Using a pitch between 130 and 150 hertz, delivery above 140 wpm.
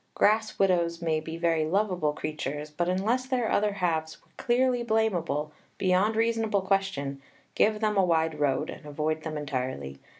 No: medium, 175 Hz; average, 160 wpm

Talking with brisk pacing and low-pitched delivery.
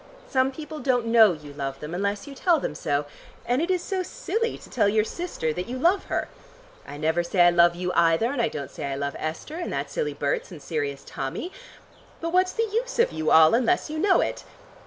No: fast, 230 wpm; high, 235 Hz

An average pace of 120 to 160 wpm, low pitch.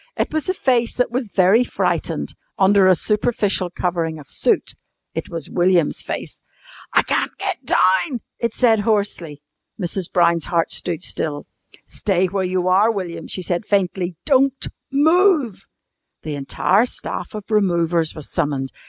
No: average, 150 wpm; high, 190 Hz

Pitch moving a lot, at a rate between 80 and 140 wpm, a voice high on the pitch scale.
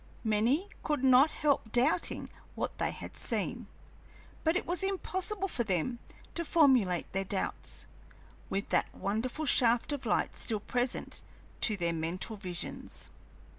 Yes: wide, 7.3 semitones; slow, 135 wpm; high, 245 Hz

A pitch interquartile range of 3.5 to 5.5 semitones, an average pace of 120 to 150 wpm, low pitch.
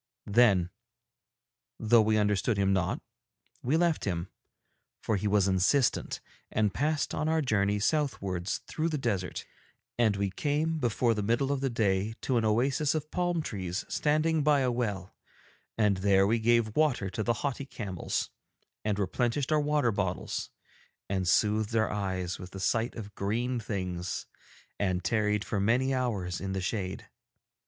No: average, 5.2 semitones; average, 160 wpm; low, 110 Hz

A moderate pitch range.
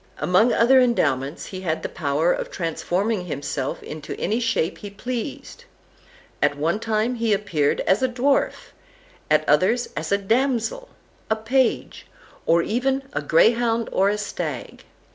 No: wide, 6.1 semitones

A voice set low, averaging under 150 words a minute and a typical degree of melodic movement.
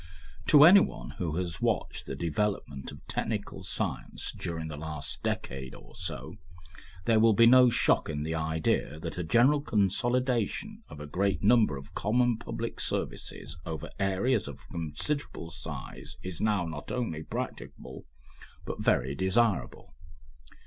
No: very low, 90 Hz; average, 140 wpm; wide, 6.9 semitones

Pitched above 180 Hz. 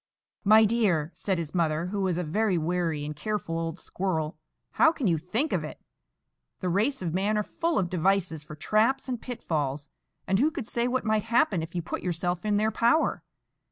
Yes: high, 190 Hz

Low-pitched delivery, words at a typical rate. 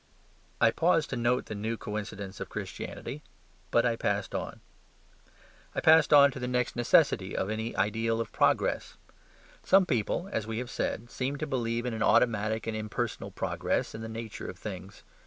Yes: low, 115 Hz; average, 175 wpm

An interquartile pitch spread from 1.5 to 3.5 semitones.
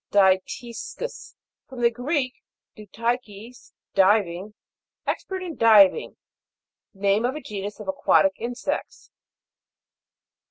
No: average, 3.9 semitones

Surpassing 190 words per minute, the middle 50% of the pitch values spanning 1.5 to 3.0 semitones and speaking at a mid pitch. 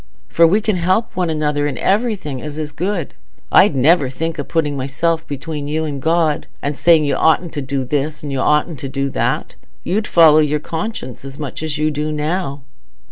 Yes: average, 200 wpm; average, 2.7 semitones; medium, 150 Hz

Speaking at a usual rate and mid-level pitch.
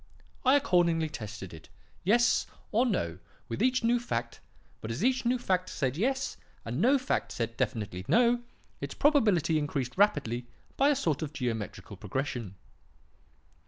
Yes: average, 150 wpm; medium, 160 Hz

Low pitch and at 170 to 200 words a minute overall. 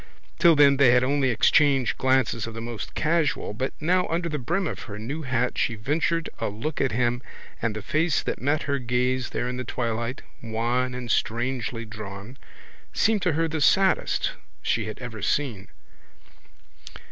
Yes: low, 125 Hz; average, 175 wpm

